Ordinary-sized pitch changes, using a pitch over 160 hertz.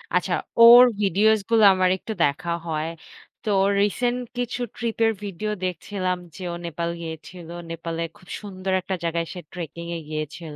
Yes: average, 4.2 semitones; medium, 185 Hz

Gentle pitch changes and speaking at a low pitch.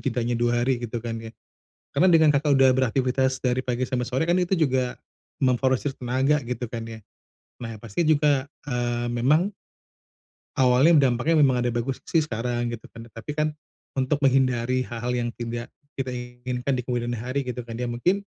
Yes: narrow, 2.1 semitones; low, 125 Hz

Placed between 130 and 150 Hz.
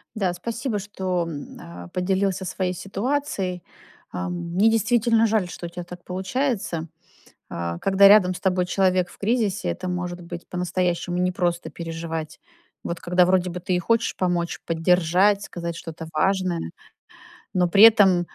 No: medium, 180 Hz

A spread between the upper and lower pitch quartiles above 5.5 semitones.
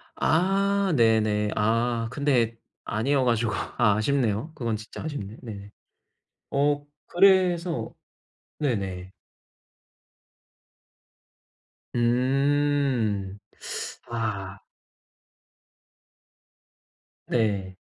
No: average, 5.2 semitones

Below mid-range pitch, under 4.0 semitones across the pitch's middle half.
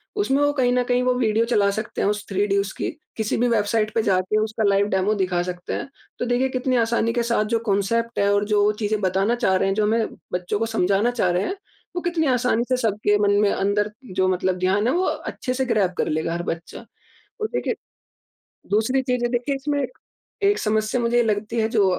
No: high, 215 Hz; average, 3.6 semitones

